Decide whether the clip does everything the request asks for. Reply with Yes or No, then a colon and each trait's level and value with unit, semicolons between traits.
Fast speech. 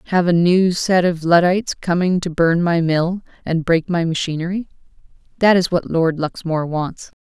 No: average, 175 wpm